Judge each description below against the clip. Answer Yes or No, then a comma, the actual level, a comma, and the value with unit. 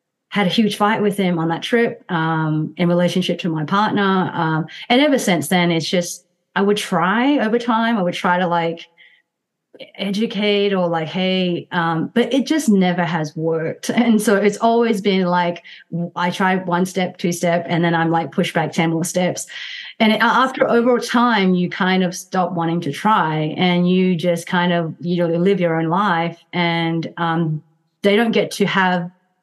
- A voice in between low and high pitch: Yes, medium, 180 Hz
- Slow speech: No, average, 190 wpm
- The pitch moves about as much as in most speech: Yes, average, 3.4 semitones